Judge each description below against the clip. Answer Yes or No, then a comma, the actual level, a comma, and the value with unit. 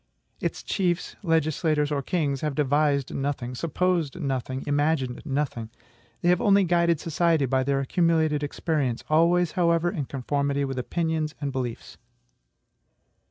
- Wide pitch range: No, average, 3.5 semitones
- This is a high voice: No, medium, 150 Hz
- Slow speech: Yes, slow, 130 wpm